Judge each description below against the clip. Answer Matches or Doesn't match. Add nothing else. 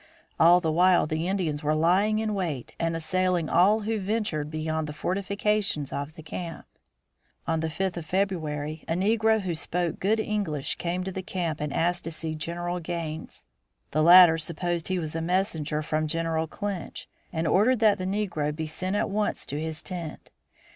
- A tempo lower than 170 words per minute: Doesn't match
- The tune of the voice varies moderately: Matches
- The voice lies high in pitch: Doesn't match